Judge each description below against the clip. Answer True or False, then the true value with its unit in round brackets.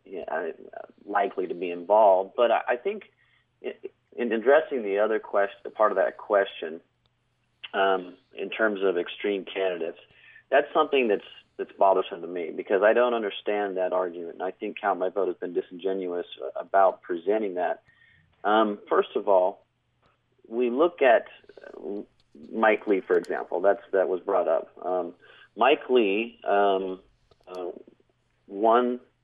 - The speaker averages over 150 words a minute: False (145 wpm)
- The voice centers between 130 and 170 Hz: False (105 Hz)